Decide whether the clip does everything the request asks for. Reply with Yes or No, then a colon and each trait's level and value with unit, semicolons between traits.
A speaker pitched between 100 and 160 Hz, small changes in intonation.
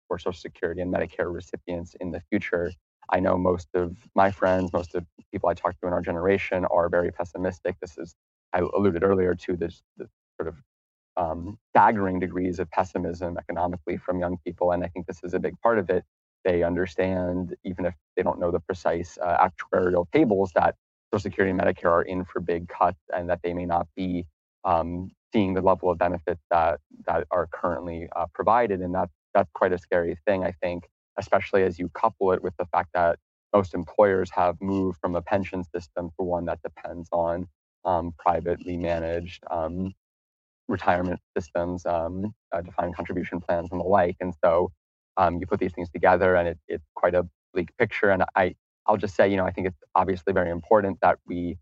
No: very low, 90 Hz; narrow, 1.3 semitones